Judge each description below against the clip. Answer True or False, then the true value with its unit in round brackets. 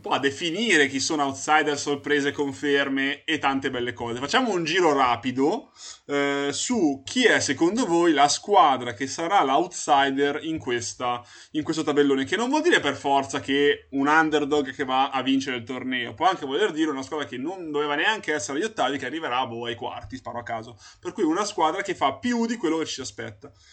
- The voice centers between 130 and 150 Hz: True (140 Hz)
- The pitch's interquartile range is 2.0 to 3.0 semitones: True (2.6 semitones)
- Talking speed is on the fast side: True (200 wpm)